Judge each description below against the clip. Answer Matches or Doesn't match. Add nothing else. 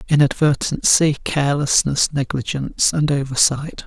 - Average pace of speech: Doesn't match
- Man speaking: Matches